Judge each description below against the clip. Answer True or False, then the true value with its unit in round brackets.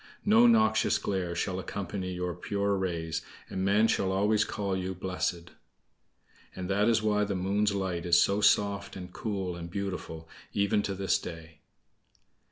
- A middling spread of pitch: False (2.2 semitones)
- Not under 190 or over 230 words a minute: False (160 wpm)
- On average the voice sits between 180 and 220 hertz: False (95 Hz)